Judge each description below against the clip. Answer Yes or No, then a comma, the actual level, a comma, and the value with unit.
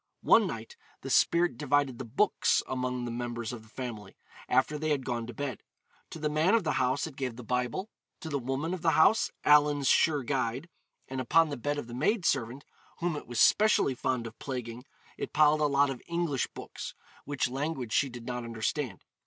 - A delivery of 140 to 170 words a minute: No, fast, 205 wpm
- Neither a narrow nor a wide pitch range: Yes, average, 3.8 semitones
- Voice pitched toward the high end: No, low, 135 Hz